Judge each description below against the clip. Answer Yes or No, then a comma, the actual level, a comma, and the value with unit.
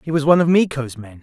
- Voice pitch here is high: No, medium, 145 Hz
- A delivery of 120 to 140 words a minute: No, fast, 295 wpm